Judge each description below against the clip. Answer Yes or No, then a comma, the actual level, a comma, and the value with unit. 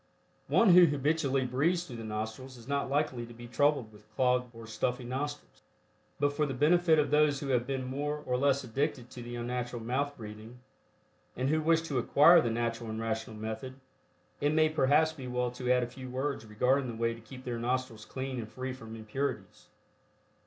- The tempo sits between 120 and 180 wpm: No, average, 200 wpm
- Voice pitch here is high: No, low, 130 Hz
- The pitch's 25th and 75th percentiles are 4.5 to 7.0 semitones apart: No, average, 3.4 semitones